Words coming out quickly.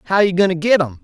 Yes: fast, 350 wpm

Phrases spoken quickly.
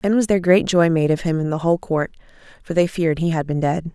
Yes: fast, 290 wpm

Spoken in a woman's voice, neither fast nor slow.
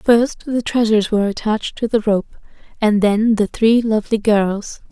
Yes: female; average, 170 wpm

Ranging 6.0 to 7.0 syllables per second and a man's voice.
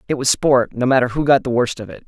Yes: 6.5 syllables/s; male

